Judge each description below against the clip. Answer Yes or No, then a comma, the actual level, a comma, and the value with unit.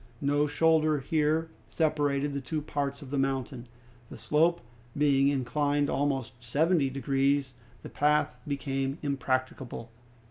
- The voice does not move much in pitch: Yes, narrow, 1.8 semitones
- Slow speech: Yes, slow, 120 wpm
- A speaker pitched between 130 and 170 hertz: Yes, medium, 140 Hz